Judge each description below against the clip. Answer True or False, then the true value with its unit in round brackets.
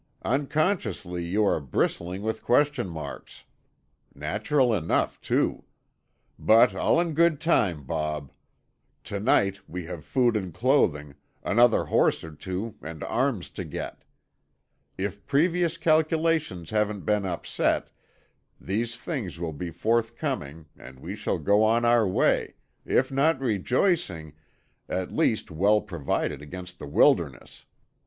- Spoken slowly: True (125 wpm)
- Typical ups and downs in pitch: False (7.4 semitones)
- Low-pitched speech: True (105 Hz)